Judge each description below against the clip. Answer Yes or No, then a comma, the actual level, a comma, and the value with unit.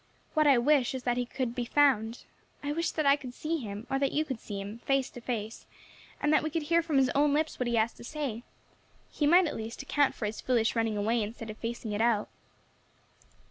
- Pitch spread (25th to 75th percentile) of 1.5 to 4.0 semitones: No, average, 4.4 semitones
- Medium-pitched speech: No, very high, 250 Hz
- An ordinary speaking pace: No, fast, 240 wpm